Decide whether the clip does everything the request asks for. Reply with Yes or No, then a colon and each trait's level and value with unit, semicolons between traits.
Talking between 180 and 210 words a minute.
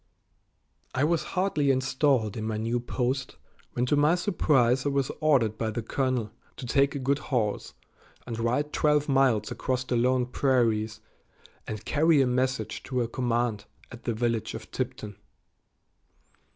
No: average, 155 wpm